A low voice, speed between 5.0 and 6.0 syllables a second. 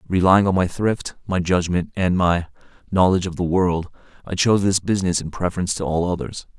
Yes: very low, 90 Hz; 5.9 syllables/s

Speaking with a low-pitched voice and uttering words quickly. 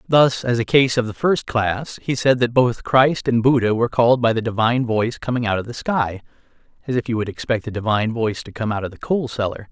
Yes: low, 120 Hz; fast, 255 wpm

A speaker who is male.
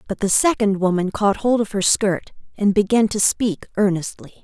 No: female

